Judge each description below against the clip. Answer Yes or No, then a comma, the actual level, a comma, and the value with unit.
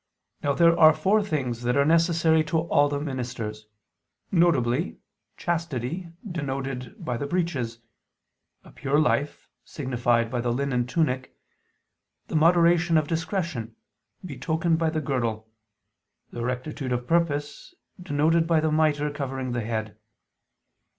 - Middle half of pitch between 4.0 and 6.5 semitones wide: Yes, average, 4.9 semitones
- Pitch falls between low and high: Yes, medium, 145 Hz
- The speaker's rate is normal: No, slow, 130 wpm